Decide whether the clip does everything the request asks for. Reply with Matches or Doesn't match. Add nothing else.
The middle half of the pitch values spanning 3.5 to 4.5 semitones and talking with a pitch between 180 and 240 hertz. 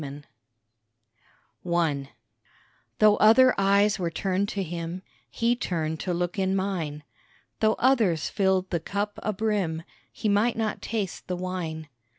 Matches